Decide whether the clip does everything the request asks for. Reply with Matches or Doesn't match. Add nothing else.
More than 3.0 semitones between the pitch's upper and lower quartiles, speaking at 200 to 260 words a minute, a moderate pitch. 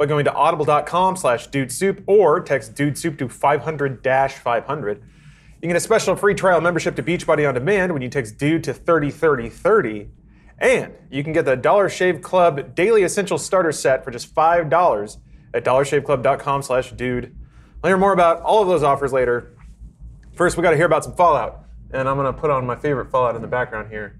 Matches